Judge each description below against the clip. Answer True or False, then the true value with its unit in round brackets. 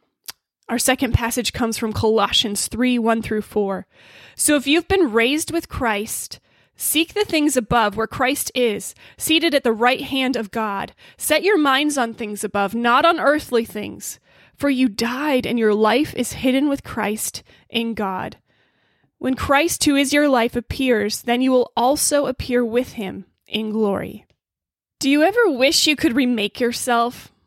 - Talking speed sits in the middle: True (170 wpm)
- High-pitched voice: True (245 Hz)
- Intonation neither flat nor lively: True (3.9 semitones)